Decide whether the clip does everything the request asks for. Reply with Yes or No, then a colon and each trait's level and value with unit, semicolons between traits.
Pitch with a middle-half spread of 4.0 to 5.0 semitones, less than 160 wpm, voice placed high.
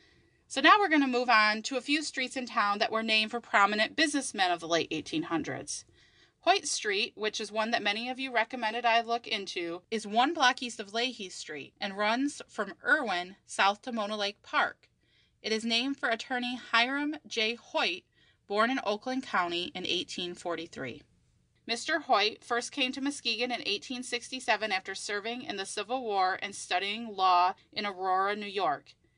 No: average, 4.3 semitones; average, 180 wpm; high, 230 Hz